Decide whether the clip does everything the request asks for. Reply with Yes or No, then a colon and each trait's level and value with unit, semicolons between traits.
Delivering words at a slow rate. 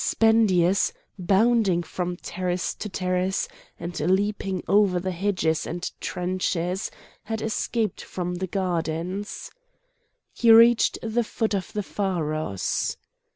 Yes: slow, 110 wpm